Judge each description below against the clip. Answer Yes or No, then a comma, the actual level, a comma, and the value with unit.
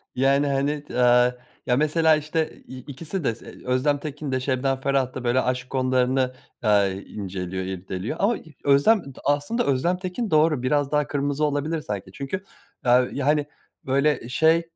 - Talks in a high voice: No, medium, 140 Hz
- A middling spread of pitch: Yes, average, 3.2 semitones